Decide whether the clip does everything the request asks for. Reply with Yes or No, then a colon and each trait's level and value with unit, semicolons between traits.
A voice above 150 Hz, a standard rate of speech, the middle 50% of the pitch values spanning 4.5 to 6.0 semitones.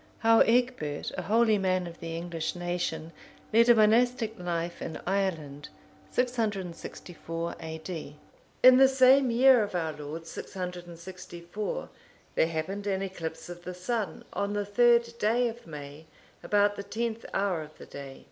Yes: high, 190 Hz; average, 145 wpm; average, 5.3 semitones